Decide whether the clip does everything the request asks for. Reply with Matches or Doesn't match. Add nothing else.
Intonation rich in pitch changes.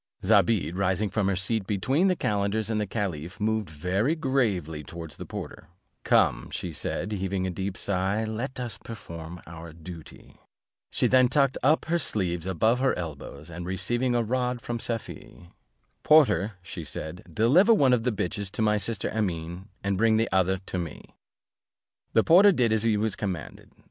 Doesn't match